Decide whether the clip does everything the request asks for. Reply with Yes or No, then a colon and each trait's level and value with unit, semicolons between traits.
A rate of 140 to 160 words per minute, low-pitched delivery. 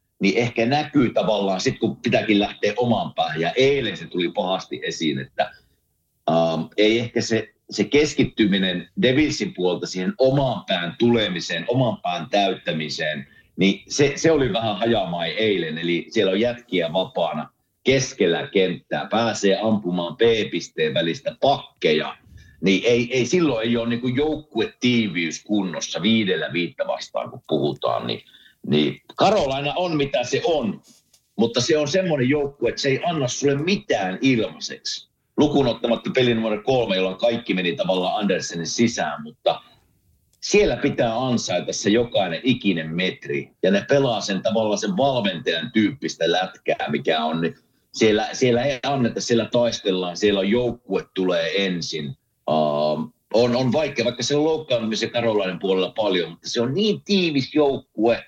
Yes: average, 145 wpm; low, 115 Hz